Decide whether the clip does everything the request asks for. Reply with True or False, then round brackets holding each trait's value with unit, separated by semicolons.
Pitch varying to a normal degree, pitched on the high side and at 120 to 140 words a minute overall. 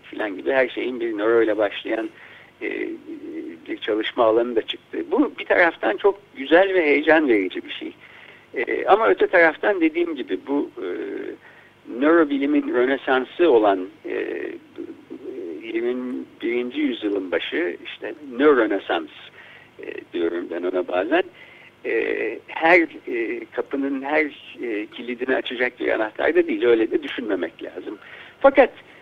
False (6.3 semitones; 345 Hz; 130 wpm)